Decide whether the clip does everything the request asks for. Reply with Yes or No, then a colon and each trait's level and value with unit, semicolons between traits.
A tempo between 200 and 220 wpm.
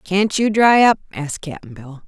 Yes: fast, 205 wpm